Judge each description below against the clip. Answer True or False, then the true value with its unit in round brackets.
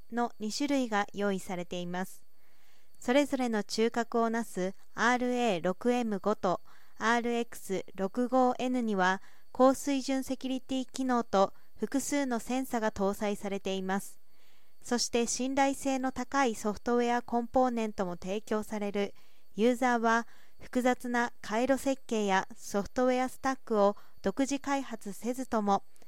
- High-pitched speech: True (235 Hz)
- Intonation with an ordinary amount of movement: True (4.0 semitones)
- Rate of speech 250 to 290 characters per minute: True (270 characters per minute)